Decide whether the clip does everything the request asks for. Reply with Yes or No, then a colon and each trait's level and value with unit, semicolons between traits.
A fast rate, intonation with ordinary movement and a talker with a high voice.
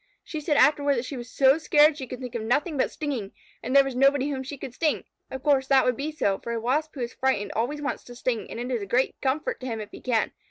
Yes: fast, 285 wpm; average, 3.1 semitones; very high, 265 Hz